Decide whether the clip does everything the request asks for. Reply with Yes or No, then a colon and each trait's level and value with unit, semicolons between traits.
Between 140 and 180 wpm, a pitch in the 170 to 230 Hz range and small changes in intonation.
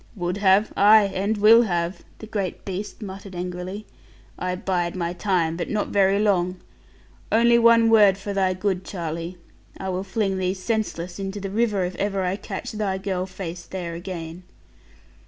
Yes: average, 170 wpm; high, 190 Hz; narrow, 2.2 semitones